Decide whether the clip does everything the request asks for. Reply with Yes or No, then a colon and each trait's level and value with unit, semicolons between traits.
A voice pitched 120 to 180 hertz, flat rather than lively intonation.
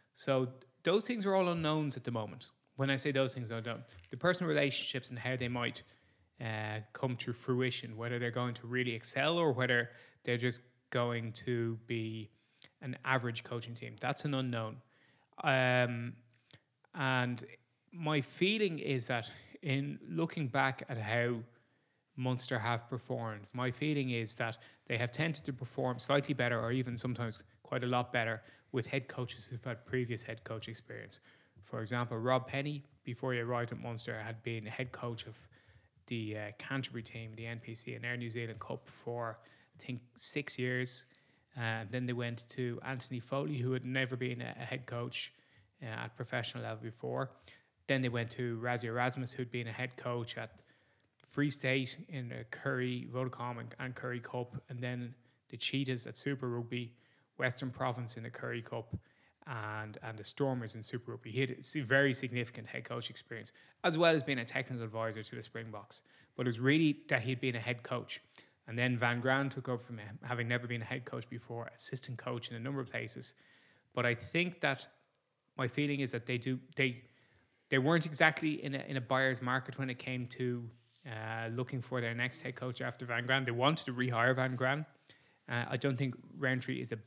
Yes: low, 125 Hz; narrow, 2.0 semitones